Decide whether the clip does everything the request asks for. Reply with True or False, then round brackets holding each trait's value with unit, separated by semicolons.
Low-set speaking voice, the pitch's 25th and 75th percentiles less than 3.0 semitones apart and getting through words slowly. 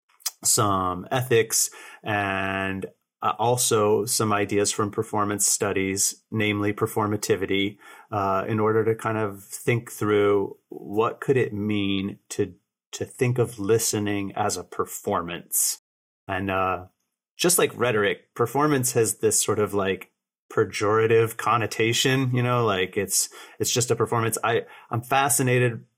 True (105 Hz; 2.6 semitones; 125 wpm)